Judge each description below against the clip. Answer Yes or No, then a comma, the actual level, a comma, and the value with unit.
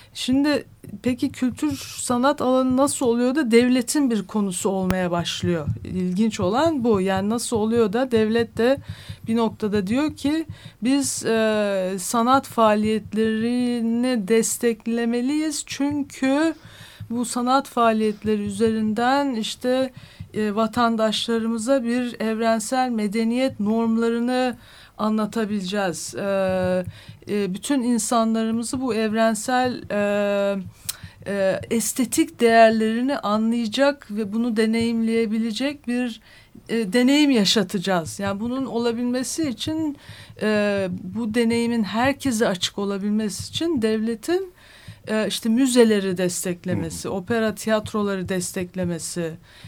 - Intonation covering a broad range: No, average, 3.3 semitones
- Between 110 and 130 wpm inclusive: No, slow, 95 wpm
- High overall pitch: Yes, high, 225 Hz